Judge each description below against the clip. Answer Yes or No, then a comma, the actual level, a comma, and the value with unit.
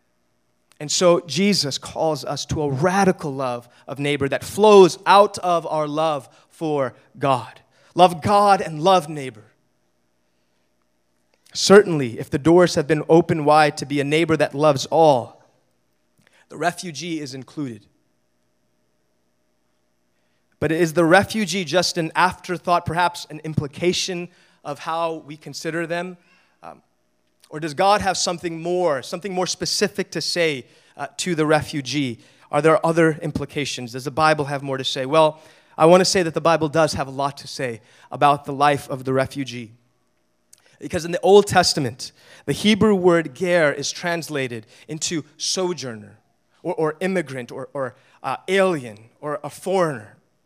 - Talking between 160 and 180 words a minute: No, average, 150 wpm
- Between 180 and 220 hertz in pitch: No, medium, 150 Hz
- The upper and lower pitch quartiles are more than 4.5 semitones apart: Yes, average, 5.1 semitones